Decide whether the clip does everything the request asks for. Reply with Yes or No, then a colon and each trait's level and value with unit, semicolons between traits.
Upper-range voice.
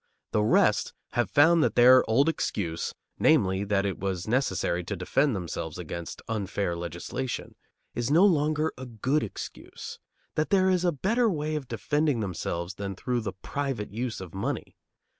No: low, 120 Hz